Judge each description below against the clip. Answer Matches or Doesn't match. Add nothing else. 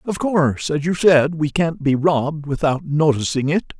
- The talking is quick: Doesn't match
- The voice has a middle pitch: Matches